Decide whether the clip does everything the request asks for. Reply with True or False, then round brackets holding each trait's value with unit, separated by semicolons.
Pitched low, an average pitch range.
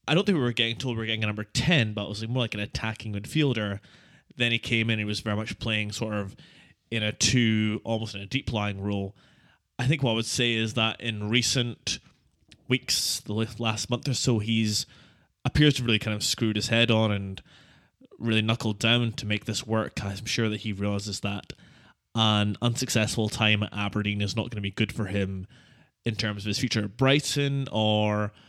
False (110 Hz; 2.2 semitones)